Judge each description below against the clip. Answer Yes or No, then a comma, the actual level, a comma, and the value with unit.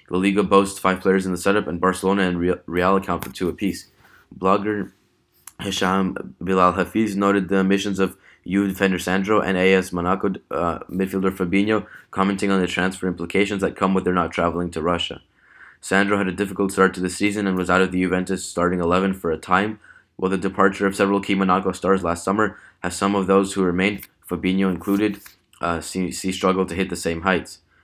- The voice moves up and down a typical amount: No, narrow, 1.5 semitones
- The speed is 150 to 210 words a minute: Yes, fast, 205 wpm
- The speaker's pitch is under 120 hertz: Yes, very low, 95 Hz